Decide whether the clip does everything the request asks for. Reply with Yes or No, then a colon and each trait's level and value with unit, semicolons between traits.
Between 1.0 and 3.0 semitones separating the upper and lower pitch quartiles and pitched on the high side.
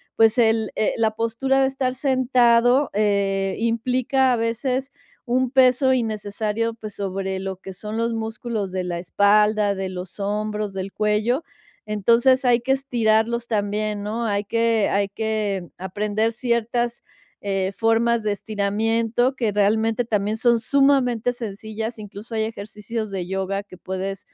Yes: average, 2.7 semitones; high, 220 Hz